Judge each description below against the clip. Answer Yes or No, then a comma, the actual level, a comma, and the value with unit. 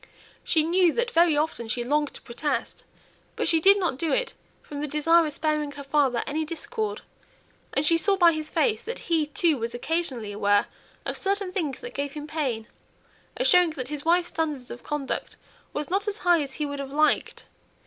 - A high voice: Yes, very high, 305 Hz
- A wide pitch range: No, average, 3.6 semitones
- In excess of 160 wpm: Yes, average, 200 wpm